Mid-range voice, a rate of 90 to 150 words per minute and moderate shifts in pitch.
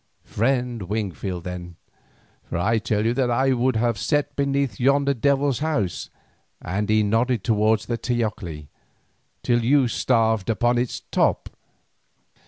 No: low, 115 Hz; slow, 135 wpm; average, 3.7 semitones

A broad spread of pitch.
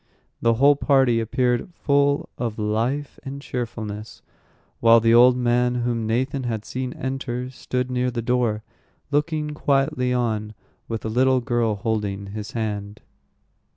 No: average, 2.8 semitones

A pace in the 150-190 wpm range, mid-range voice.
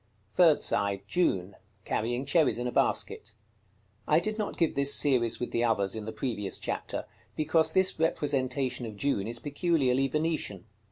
No: average, 160 wpm; low, 130 Hz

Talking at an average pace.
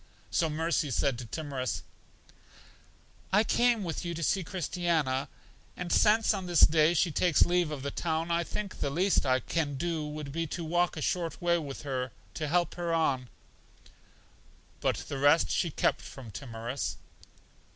Yes: average, 170 wpm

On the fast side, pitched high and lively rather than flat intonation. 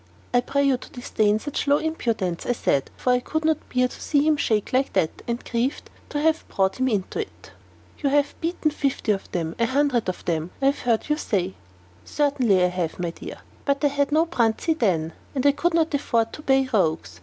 Yes: fast, 220 wpm; very high, 255 Hz; wide, 6.2 semitones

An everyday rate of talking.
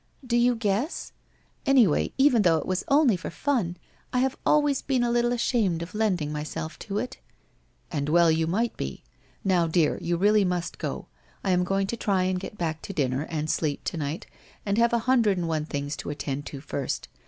No: fast, 210 wpm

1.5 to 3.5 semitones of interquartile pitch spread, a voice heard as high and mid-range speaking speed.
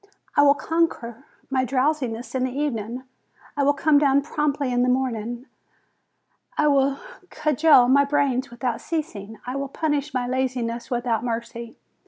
Yes: average, 2.9 semitones; very high, 260 Hz; average, 150 wpm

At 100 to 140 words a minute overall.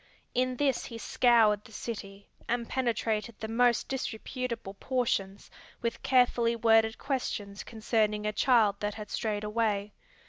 Yes: slow, 135 wpm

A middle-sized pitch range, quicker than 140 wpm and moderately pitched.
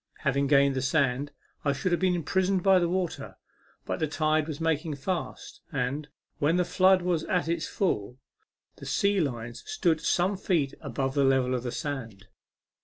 Yes: average, 4.7 semitones; average, 180 wpm; medium, 155 Hz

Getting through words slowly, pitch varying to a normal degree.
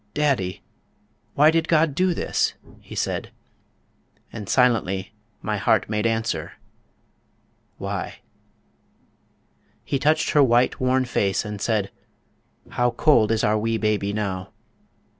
Yes: slow, 120 wpm; average, 4.4 semitones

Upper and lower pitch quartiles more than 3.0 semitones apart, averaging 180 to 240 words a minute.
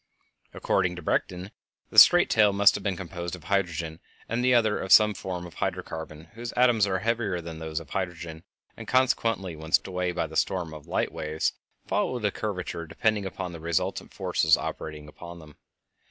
Yes: average, 4.0 semitones; average, 195 wpm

